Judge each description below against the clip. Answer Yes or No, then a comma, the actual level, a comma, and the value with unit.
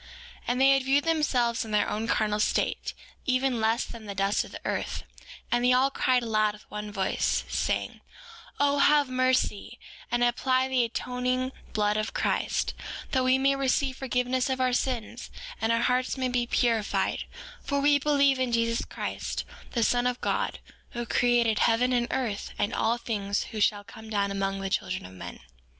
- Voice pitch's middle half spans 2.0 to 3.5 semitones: Yes, average, 3.0 semitones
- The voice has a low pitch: No, high, 245 Hz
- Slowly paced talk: No, average, 185 wpm